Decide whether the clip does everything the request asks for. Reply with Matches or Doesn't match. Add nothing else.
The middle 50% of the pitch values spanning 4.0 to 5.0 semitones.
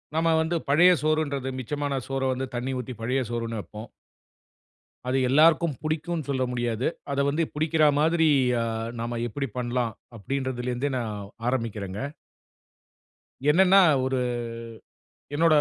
Matches